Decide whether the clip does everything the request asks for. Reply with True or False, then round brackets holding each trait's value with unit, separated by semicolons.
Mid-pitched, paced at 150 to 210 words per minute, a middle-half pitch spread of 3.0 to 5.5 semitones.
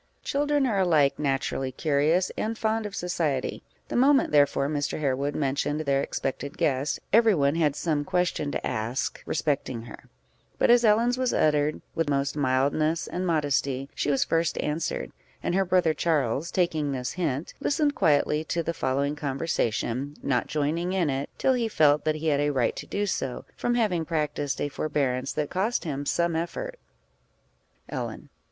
True (150 Hz; 170 wpm; 4.2 semitones)